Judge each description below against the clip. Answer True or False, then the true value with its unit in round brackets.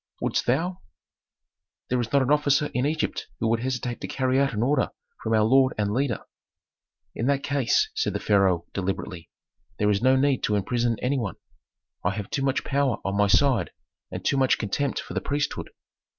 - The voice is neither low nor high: False (125 Hz)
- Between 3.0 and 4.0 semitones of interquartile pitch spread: False (4.7 semitones)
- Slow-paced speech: False (195 wpm)